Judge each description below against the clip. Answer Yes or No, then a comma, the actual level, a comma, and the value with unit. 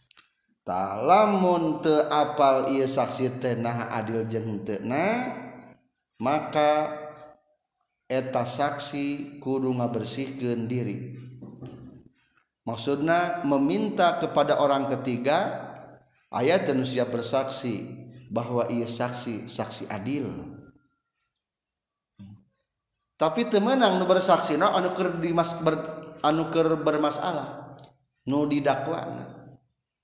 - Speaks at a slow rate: Yes, slow, 70 wpm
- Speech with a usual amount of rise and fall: Yes, average, 4.4 semitones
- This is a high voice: No, medium, 140 Hz